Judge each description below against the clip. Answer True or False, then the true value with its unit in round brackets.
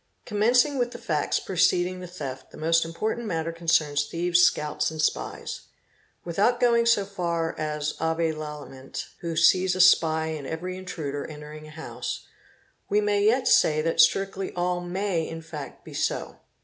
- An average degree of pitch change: True (3.4 semitones)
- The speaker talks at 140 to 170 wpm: True (165 wpm)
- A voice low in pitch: False (165 Hz)